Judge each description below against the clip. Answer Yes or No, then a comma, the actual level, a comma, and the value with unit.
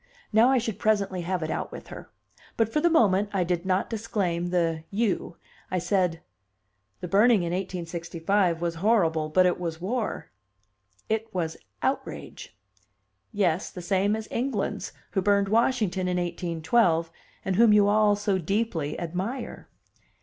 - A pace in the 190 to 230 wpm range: No, average, 155 wpm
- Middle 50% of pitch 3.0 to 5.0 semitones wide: Yes, average, 3.8 semitones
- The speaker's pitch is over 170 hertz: Yes, high, 190 Hz